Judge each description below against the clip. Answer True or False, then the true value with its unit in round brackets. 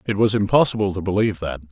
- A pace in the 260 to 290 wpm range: False (210 wpm)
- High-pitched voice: False (100 Hz)